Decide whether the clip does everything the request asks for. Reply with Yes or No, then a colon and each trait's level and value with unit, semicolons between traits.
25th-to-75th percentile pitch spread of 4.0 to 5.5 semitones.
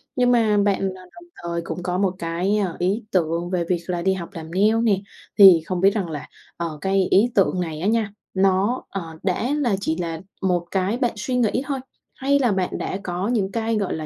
No: average, 3.5 semitones